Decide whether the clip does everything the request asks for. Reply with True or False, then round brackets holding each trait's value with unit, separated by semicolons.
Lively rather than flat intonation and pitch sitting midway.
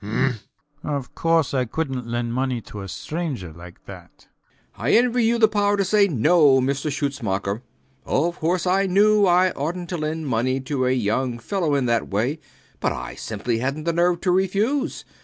True (6.6 semitones; 145 Hz)